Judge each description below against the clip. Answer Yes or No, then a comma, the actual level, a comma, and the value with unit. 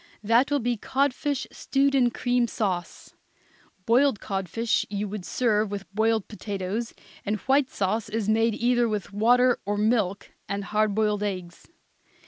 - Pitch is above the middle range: Yes, high, 220 Hz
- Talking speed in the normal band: Yes, average, 150 wpm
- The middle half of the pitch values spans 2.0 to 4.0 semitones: Yes, average, 3.2 semitones